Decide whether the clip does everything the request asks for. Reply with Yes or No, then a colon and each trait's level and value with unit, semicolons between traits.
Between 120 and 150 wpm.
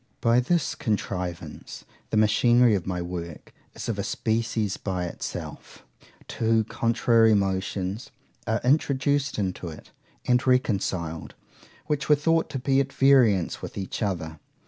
Yes: slow, 135 wpm